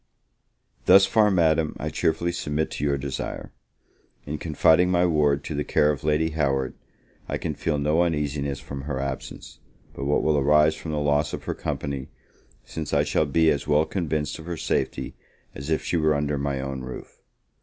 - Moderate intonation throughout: No, narrow, 2.0 semitones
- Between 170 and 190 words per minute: Yes, average, 185 wpm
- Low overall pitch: Yes, very low, 75 Hz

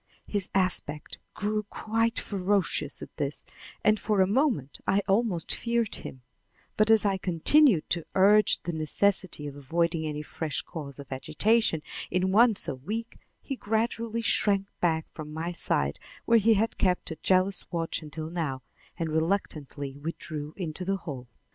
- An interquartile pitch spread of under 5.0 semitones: No, average, 5.3 semitones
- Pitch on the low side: No, medium, 185 Hz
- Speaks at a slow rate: No, average, 155 wpm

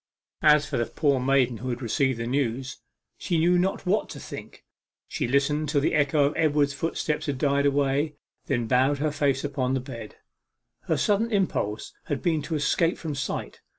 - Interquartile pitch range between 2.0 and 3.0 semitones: Yes, average, 2.7 semitones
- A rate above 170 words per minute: Yes, average, 185 wpm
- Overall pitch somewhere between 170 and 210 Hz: No, medium, 140 Hz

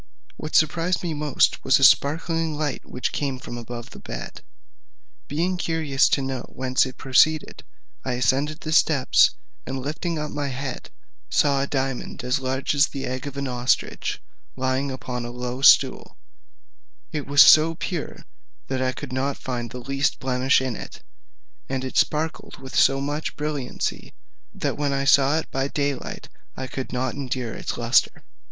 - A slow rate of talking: No, average, 170 wpm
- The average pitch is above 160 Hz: No, low, 135 Hz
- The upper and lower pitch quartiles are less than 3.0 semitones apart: Yes, narrow, 2.4 semitones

